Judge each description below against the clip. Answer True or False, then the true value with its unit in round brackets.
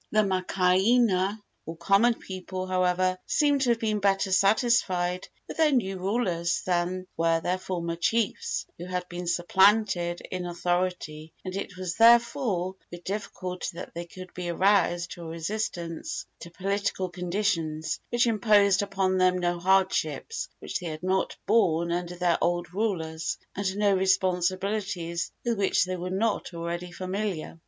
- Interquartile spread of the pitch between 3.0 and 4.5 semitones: False (2.5 semitones)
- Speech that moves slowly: False (150 wpm)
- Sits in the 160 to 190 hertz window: True (185 Hz)